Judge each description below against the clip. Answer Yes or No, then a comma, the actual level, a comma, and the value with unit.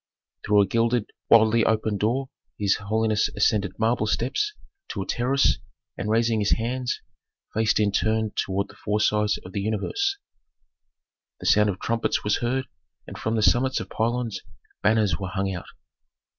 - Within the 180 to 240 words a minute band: No, average, 160 wpm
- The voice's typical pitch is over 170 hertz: No, low, 110 Hz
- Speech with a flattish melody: Yes, narrow, 2.1 semitones